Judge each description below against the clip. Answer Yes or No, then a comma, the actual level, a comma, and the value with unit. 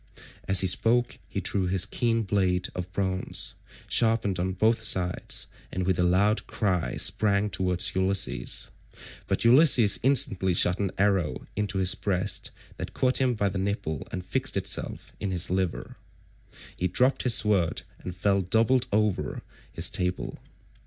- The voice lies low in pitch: Yes, very low, 95 Hz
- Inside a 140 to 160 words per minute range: Yes, average, 155 wpm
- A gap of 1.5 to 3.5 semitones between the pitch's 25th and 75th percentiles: Yes, average, 2.8 semitones